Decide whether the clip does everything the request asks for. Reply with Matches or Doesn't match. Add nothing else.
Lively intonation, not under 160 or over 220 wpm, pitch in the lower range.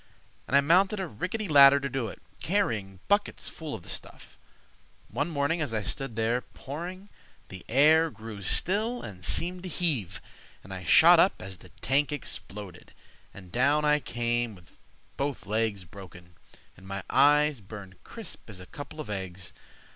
Matches